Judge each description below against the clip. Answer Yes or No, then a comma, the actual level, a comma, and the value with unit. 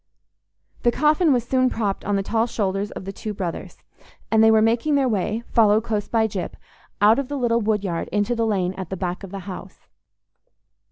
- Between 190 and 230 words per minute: Yes, fast, 205 wpm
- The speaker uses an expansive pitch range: No, average, 3.1 semitones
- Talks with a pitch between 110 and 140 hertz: No, high, 220 Hz